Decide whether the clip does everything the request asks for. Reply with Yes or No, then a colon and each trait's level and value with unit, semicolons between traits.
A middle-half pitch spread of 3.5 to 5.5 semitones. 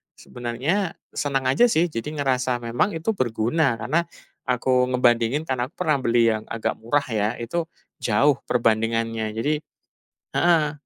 Yes: average, 4.5 semitones